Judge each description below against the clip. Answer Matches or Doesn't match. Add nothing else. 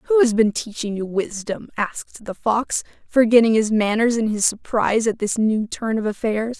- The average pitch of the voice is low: Doesn't match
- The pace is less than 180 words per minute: Doesn't match